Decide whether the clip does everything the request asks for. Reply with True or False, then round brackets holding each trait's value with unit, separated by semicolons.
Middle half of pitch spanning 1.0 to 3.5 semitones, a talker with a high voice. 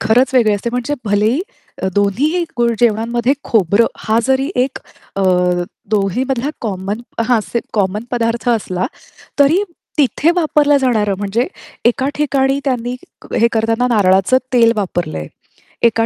False (4.0 semitones; 235 Hz)